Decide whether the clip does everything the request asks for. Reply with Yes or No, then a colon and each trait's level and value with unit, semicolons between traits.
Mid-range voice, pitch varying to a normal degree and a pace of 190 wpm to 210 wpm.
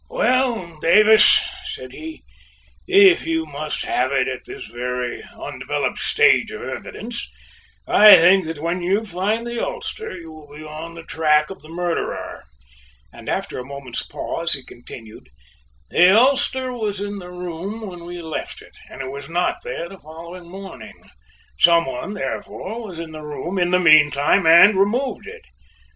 No: medium, 170 Hz; average, 4.8 semitones; average, 165 wpm